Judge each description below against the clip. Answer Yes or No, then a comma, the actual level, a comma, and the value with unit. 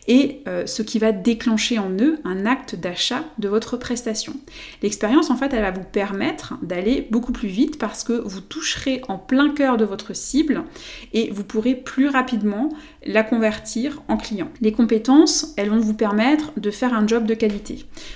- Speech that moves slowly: No, average, 180 wpm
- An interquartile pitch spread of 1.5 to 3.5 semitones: No, average, 4.2 semitones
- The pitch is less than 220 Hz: No, high, 235 Hz